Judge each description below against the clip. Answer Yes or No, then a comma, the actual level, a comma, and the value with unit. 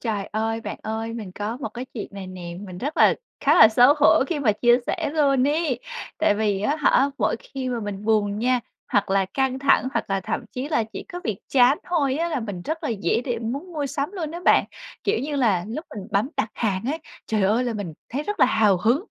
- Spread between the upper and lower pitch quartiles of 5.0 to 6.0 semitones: Yes, average, 5.3 semitones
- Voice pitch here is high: Yes, high, 235 Hz